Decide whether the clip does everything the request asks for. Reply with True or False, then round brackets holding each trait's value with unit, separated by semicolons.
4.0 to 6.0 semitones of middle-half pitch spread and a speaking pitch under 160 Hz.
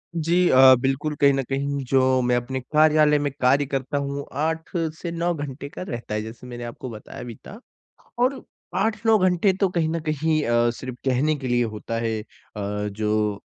True (4.4 semitones; 140 Hz)